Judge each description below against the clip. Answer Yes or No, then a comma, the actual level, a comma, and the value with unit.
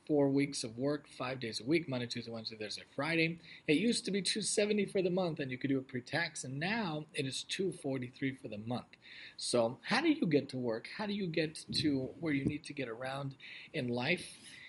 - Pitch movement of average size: Yes, average, 4.9 semitones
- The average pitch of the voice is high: No, medium, 140 Hz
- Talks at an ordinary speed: No, fast, 235 wpm